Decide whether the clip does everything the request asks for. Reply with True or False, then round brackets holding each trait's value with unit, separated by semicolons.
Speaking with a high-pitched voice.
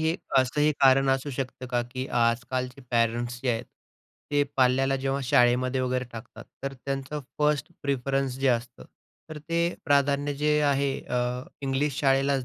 False (135 Hz)